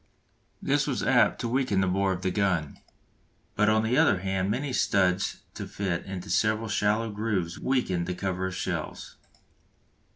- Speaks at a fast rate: No, average, 170 wpm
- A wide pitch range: No, average, 3.1 semitones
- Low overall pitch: Yes, low, 100 Hz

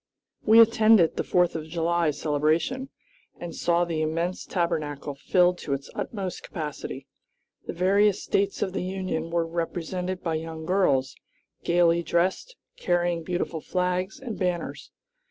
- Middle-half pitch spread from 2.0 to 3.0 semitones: Yes, narrow, 2.4 semitones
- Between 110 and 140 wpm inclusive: Yes, slow, 135 wpm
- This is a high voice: No, medium, 175 Hz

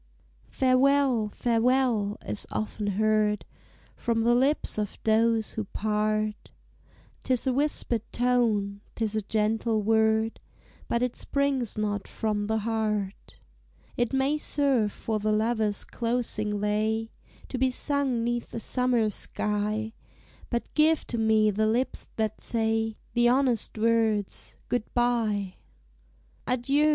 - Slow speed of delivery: Yes, slow, 125 wpm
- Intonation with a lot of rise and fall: No, narrow, 2.5 semitones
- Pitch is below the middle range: No, high, 225 Hz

